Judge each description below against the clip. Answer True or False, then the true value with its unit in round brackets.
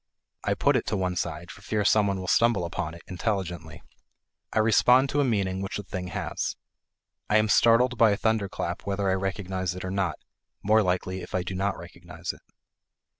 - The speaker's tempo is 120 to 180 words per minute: False (200 wpm)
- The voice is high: False (95 Hz)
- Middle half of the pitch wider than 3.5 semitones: False (3.0 semitones)